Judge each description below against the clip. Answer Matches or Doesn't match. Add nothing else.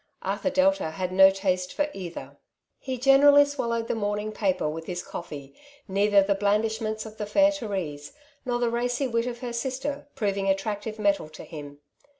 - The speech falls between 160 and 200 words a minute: Matches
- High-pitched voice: Matches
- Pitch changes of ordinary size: Matches